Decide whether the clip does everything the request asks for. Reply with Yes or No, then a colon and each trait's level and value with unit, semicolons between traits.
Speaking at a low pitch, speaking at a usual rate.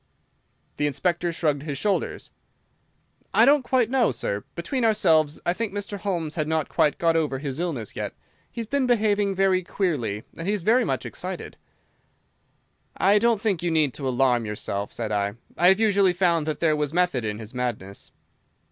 No: medium, 170 Hz; average, 175 wpm